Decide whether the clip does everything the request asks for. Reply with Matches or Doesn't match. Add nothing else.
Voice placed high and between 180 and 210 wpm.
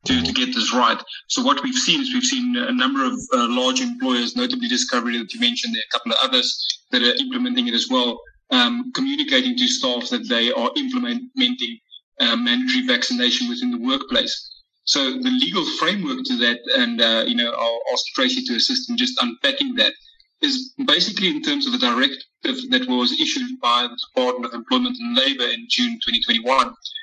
Matches